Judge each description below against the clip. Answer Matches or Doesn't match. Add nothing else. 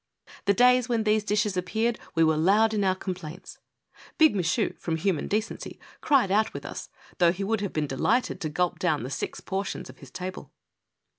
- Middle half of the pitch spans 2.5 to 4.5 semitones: Matches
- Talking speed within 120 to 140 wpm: Doesn't match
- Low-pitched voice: Doesn't match